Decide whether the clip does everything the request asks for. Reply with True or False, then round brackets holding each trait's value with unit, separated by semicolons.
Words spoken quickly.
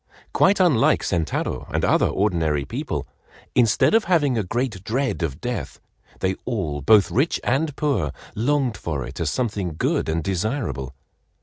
False (150 wpm)